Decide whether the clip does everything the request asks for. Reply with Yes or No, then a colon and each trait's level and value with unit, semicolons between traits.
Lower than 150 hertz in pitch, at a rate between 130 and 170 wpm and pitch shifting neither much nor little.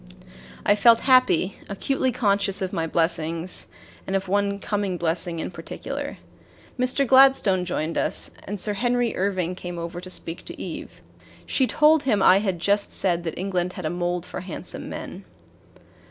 No: high, 190 Hz; average, 165 wpm; average, 3.0 semitones